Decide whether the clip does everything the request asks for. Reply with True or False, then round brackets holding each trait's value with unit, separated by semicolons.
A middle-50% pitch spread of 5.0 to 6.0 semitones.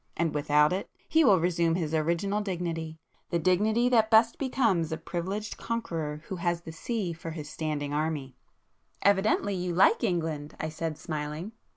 False (4.2 semitones)